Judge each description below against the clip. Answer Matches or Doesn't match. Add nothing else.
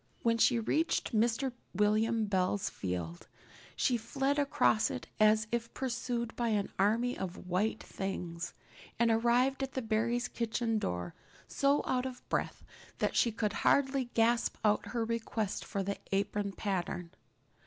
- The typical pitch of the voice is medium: Doesn't match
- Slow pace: Doesn't match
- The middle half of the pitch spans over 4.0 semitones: Doesn't match